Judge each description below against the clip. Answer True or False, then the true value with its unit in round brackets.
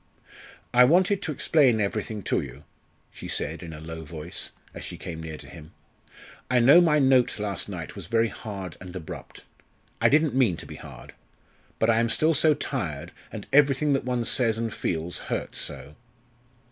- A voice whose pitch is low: True (110 Hz)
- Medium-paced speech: True (185 wpm)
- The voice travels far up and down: True (7.9 semitones)